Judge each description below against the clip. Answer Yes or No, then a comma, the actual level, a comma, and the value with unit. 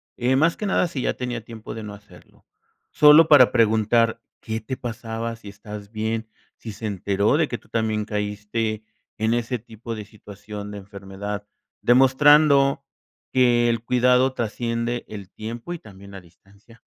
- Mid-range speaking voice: No, low, 115 Hz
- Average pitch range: Yes, average, 3.0 semitones